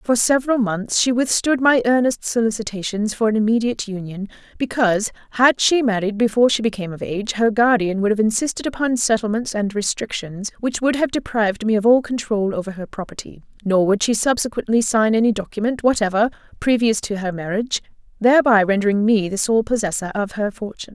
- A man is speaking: No, female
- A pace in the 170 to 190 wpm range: Yes, average, 180 wpm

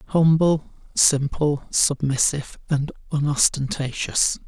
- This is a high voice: No, medium, 145 Hz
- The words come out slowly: Yes, slow, 65 wpm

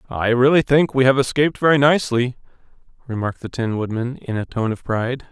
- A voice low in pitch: Yes, low, 125 Hz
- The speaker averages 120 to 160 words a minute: No, average, 190 wpm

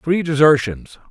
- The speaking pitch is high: No, medium, 145 Hz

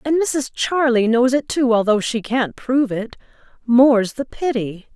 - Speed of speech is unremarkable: Yes, average, 155 wpm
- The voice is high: Yes, high, 245 Hz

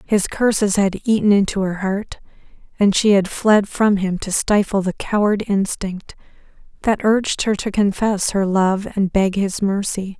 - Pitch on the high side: Yes, high, 200 Hz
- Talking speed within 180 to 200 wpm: No, average, 170 wpm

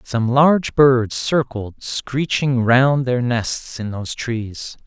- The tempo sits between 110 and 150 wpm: Yes, slow, 135 wpm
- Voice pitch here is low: Yes, low, 125 Hz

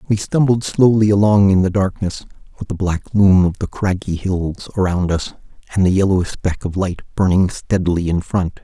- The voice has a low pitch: Yes, very low, 95 Hz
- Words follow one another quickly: No, average, 190 wpm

